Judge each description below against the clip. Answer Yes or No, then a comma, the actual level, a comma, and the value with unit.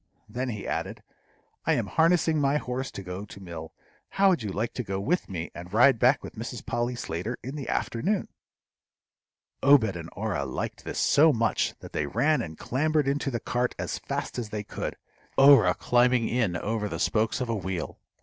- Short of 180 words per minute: No, average, 195 wpm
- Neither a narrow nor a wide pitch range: No, wide, 5.7 semitones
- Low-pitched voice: Yes, low, 120 Hz